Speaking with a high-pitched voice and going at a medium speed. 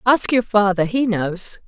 Yes: high, 210 Hz; average, 180 wpm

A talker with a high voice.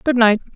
Yes: high, 235 Hz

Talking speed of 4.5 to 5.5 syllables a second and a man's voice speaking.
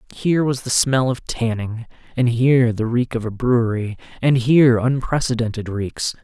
Yes: 5.0 syllables/s; male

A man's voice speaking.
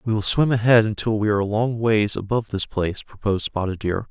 Yes: male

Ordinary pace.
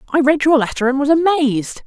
No: fast, 225 wpm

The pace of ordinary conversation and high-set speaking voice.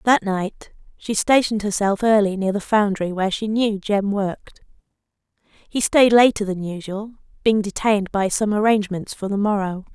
Yes: average, 165 wpm; high, 205 Hz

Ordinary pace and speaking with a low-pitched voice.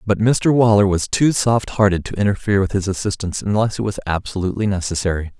Yes: average, 190 wpm; low, 100 Hz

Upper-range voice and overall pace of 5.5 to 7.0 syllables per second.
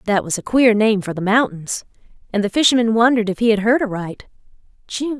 Yes: high, 220 Hz; 5.9 syllables/s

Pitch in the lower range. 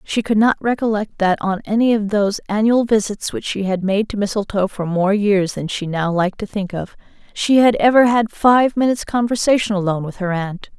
No: high, 210 Hz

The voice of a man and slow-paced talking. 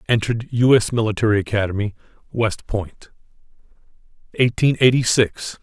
Yes: male; slow, 105 wpm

